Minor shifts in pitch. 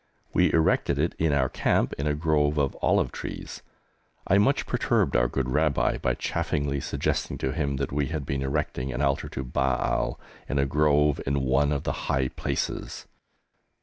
Yes: narrow, 1.9 semitones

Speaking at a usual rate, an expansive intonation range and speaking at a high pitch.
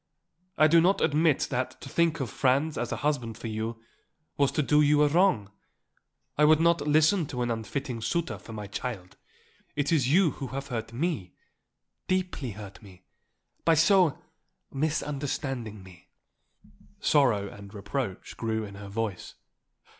No: average, 155 wpm; wide, 5.7 semitones; low, 135 Hz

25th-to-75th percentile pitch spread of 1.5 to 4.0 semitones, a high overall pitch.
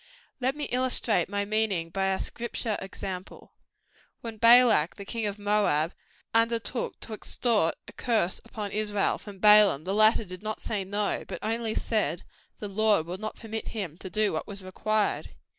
Yes: narrow, 2.5 semitones; high, 210 Hz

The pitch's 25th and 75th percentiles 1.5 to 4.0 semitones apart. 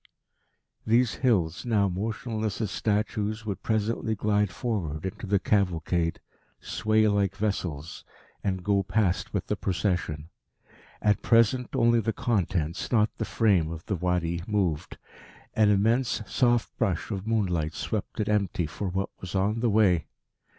Yes: average, 3.5 semitones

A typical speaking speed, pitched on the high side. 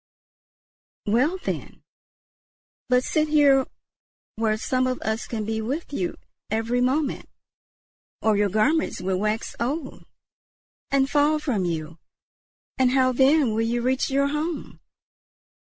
No: slow, 125 wpm; very high, 255 Hz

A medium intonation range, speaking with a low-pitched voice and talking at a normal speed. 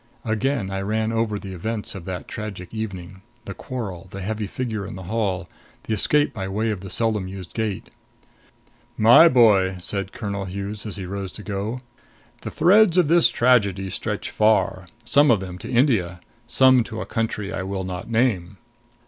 Yes: average, 3.1 semitones; low, 105 Hz; average, 180 wpm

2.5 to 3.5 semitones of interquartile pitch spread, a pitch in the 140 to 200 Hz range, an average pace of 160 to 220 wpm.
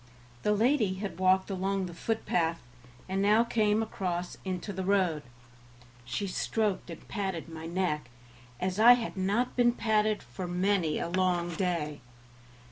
No: average, 3.2 semitones; high, 190 Hz; average, 145 wpm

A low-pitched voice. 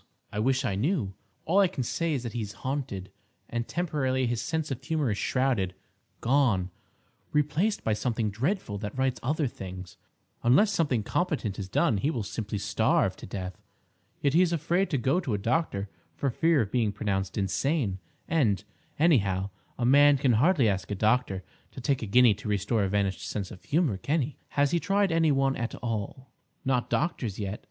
Yes: low, 125 Hz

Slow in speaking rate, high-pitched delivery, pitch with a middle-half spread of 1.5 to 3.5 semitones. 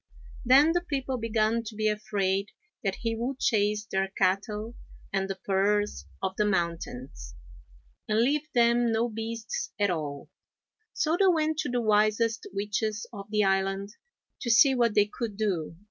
No: average, 160 wpm; high, 215 Hz; average, 3.1 semitones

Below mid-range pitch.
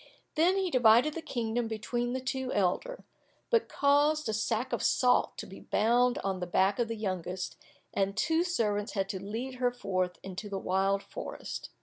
No: high, 230 Hz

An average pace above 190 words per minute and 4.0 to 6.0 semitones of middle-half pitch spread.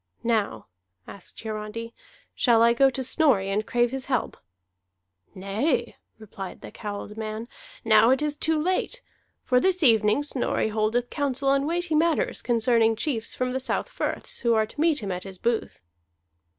No: average, 165 wpm; average, 4.3 semitones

